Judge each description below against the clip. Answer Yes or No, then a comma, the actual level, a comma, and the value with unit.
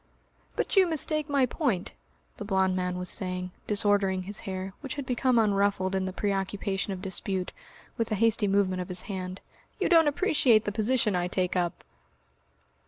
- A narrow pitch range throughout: No, average, 3.8 semitones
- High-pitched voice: Yes, high, 200 Hz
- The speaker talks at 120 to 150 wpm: No, average, 170 wpm